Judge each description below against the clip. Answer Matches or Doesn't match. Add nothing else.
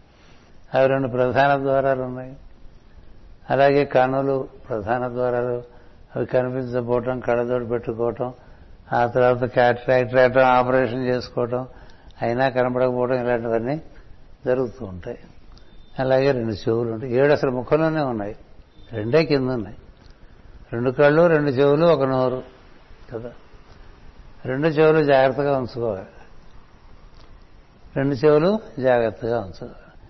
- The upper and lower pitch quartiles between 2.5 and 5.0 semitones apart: Doesn't match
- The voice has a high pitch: Doesn't match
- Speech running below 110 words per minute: Matches